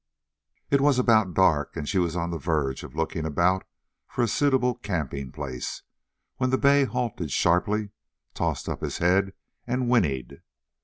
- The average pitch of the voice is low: Yes, very low, 95 Hz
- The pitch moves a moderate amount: No, wide, 7.9 semitones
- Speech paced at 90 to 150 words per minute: No, average, 160 wpm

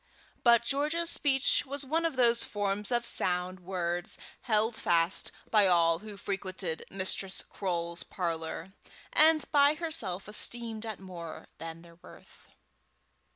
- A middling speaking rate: No, slow, 130 wpm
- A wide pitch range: Yes, wide, 5.8 semitones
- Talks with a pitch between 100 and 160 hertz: No, high, 200 Hz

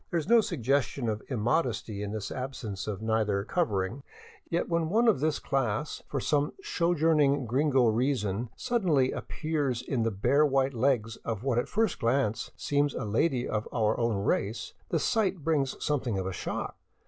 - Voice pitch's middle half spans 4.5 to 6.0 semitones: Yes, wide, 5.4 semitones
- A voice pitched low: Yes, low, 130 Hz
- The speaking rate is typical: Yes, average, 170 wpm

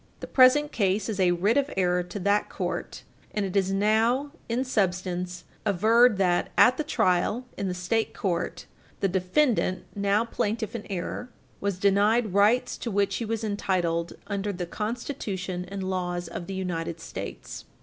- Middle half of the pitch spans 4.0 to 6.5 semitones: No, average, 3.6 semitones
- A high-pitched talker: Yes, high, 200 Hz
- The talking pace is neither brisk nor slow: Yes, average, 165 wpm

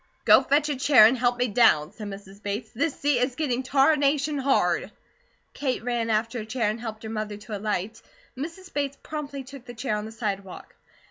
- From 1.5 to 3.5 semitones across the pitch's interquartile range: No, average, 4.5 semitones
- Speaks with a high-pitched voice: Yes, high, 245 Hz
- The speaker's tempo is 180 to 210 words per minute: Yes, average, 200 wpm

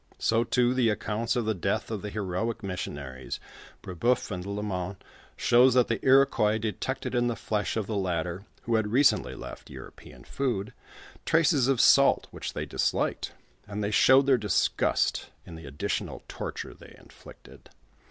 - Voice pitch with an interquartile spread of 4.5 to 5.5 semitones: No, average, 4.0 semitones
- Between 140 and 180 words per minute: Yes, average, 160 wpm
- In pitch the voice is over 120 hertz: No, low, 110 Hz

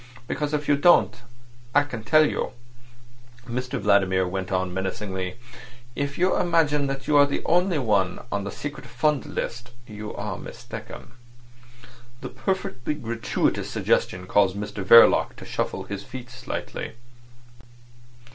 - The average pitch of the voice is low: Yes, low, 120 Hz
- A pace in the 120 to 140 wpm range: Yes, slow, 135 wpm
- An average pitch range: No, wide, 6.4 semitones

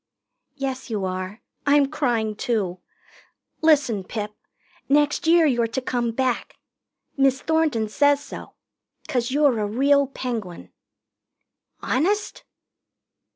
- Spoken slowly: Yes, slow, 110 wpm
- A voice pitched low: No, very high, 255 Hz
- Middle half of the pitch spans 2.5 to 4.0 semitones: No, average, 4.6 semitones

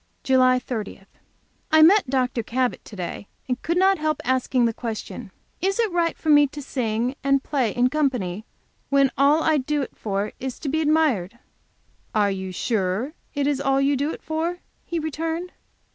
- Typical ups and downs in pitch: Yes, average, 4.8 semitones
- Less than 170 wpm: No, average, 180 wpm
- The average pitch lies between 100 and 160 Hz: No, very high, 270 Hz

